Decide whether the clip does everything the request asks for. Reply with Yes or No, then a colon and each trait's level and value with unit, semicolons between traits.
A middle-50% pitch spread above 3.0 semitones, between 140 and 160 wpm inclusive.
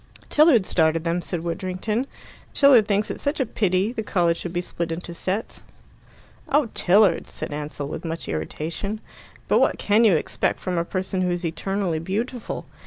No: average, 4.2 semitones; average, 170 wpm